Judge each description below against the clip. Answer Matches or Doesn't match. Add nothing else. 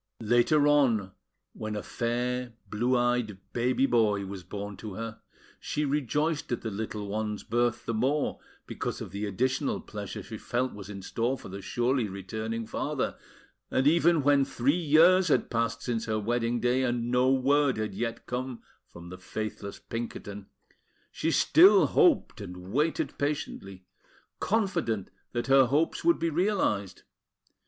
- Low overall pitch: Matches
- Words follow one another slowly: Doesn't match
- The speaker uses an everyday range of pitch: Matches